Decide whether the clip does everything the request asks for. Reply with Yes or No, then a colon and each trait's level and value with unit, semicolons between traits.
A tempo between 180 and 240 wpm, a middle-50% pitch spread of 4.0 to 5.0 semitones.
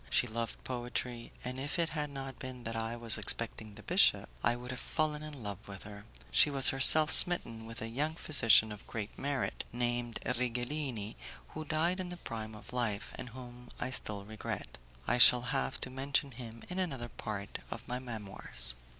No: average, 190 wpm; average, 3.4 semitones